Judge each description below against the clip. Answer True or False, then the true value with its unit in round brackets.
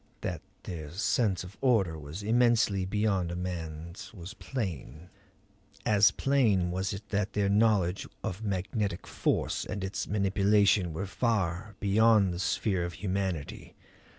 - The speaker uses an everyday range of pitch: True (3.1 semitones)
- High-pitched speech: False (95 Hz)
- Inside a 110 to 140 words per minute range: True (135 wpm)